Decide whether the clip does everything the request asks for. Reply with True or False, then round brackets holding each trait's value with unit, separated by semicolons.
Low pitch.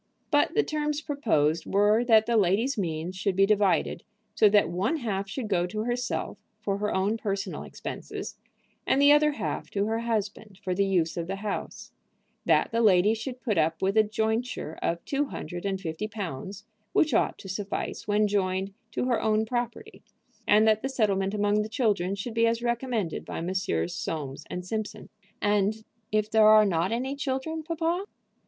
False (210 Hz)